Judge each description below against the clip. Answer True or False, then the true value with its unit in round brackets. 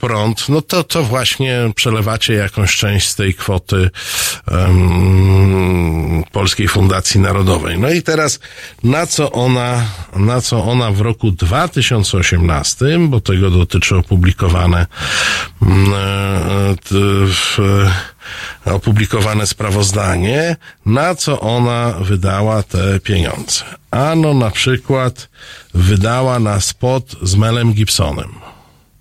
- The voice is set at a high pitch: False (105 Hz)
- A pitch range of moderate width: True (4.2 semitones)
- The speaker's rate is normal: False (105 wpm)